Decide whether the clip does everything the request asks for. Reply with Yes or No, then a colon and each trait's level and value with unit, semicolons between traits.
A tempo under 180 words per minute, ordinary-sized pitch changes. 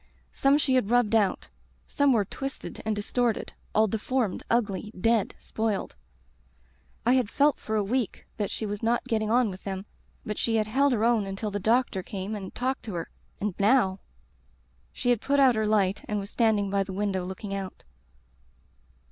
No: average, 190 wpm; average, 3.3 semitones